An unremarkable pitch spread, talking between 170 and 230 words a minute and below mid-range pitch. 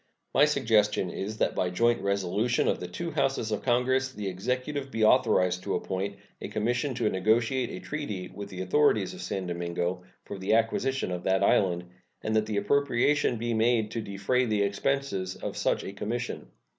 Yes: average, 4.7 semitones; average, 180 wpm; low, 110 Hz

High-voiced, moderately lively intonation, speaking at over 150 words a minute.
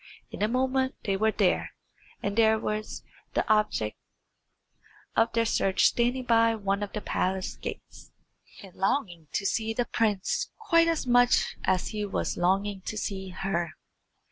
Yes: high, 215 Hz; average, 3.4 semitones; average, 160 wpm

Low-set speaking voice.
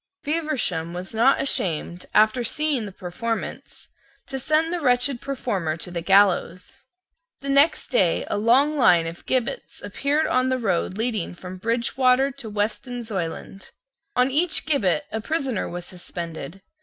No: high, 230 Hz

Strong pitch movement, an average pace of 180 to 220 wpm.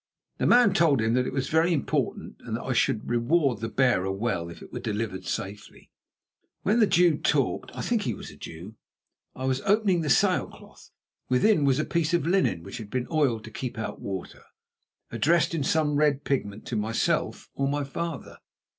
Yes: wide, 6.5 semitones; average, 200 wpm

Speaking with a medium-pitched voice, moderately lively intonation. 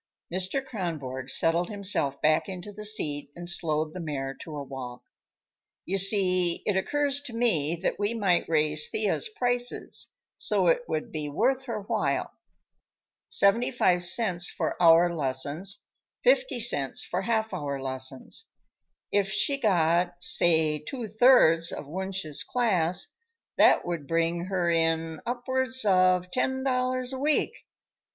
No: medium, 180 Hz; wide, 6.3 semitones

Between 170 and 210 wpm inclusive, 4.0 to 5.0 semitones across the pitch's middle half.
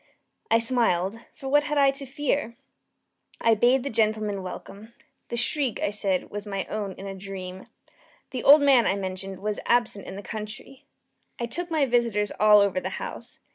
Yes: average, 180 wpm; average, 4.5 semitones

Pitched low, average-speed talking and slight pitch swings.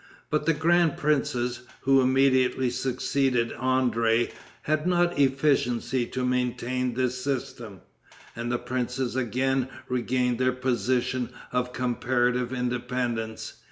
No: low, 125 Hz; slow, 110 wpm; narrow, 1.4 semitones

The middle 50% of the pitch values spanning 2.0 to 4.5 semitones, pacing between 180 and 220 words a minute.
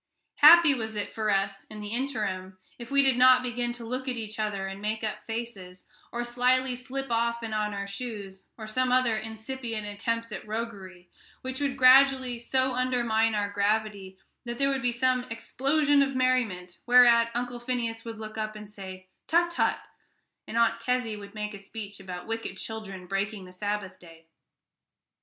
Yes: average, 3.4 semitones; average, 185 wpm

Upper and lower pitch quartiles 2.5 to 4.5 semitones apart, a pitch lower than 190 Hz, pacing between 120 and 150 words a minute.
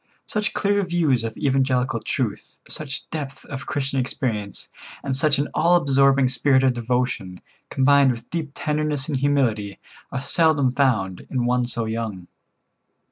Yes: average, 2.9 semitones; low, 135 Hz; average, 145 wpm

